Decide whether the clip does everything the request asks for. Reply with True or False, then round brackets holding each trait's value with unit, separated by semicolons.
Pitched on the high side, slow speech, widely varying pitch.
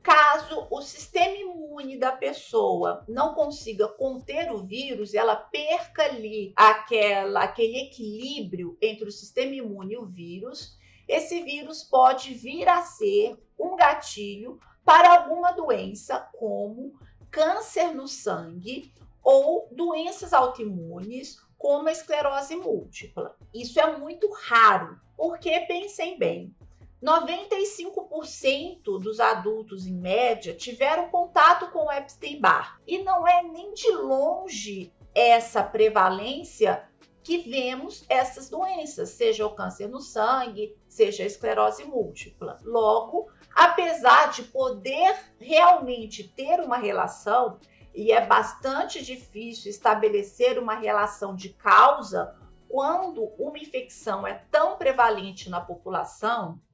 True (270 Hz; 115 wpm; 7.7 semitones)